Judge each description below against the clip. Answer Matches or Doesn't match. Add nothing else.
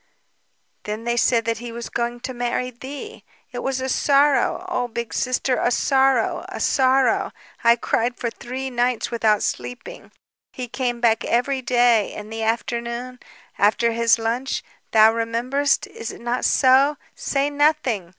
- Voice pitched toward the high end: Matches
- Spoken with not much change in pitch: Matches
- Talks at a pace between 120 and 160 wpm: Matches